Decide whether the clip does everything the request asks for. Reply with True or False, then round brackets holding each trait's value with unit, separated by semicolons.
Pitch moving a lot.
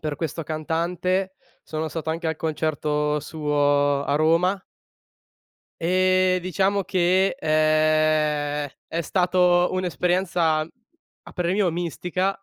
False (2.9 semitones)